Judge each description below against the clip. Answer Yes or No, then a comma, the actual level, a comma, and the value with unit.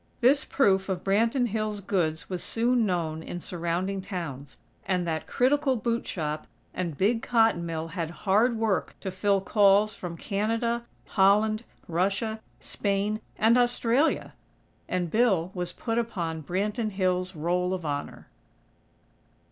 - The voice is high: Yes, high, 195 Hz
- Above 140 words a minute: No, slow, 135 wpm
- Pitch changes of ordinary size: Yes, average, 4.3 semitones